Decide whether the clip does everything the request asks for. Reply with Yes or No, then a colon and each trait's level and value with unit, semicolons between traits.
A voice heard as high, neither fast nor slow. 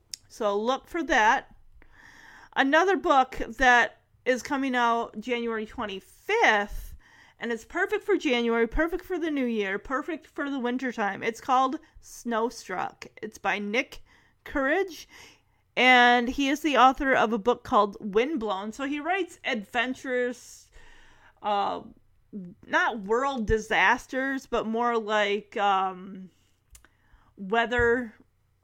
No: high, 245 Hz; slow, 115 wpm